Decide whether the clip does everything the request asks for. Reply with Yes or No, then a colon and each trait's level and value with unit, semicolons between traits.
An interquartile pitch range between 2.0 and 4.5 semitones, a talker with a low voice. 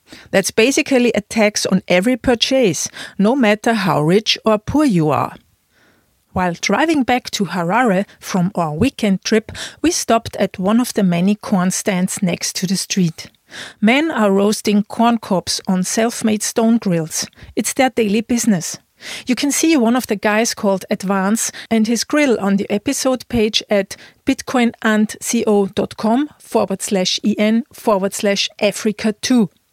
No: average, 3.3 semitones; high, 215 Hz